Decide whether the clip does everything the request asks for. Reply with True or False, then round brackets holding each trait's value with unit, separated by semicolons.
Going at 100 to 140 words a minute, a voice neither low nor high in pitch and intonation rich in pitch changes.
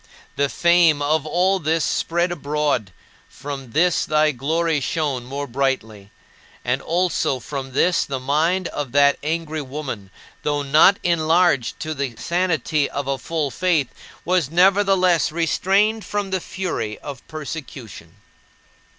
False (135 wpm; 155 Hz; 3.9 semitones)